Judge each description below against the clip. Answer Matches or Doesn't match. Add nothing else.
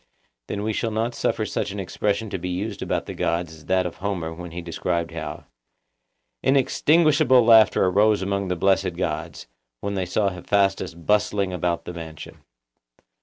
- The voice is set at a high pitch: Doesn't match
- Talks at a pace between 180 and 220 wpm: Doesn't match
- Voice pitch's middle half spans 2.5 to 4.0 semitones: Matches